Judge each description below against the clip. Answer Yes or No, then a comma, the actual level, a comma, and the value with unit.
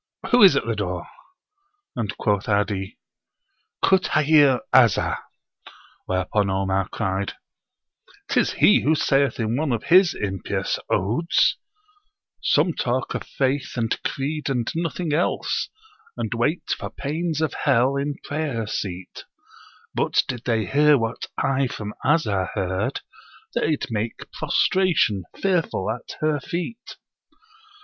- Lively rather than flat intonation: Yes, wide, 6.7 semitones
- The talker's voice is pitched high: No, low, 130 Hz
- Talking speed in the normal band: No, slow, 125 wpm